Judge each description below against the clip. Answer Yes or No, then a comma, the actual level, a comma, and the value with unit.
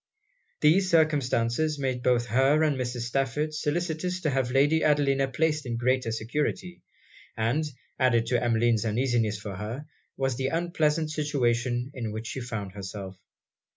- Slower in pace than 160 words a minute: Yes, average, 145 wpm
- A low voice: Yes, low, 130 Hz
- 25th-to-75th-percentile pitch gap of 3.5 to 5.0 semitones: Yes, average, 4.4 semitones